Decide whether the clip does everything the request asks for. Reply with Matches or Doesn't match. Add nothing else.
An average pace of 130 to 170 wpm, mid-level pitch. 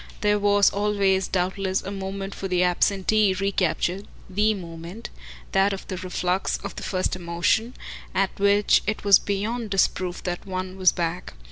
Doesn't match